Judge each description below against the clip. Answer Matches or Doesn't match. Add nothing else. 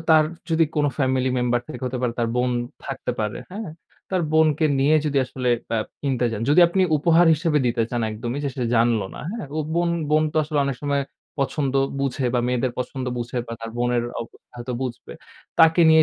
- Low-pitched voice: Matches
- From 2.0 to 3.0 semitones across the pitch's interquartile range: Doesn't match